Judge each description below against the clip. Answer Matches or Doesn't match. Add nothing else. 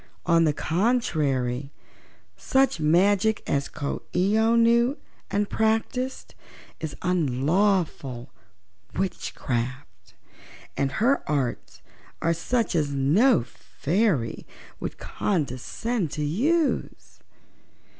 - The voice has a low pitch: Doesn't match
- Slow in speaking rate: Matches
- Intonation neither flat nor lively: Doesn't match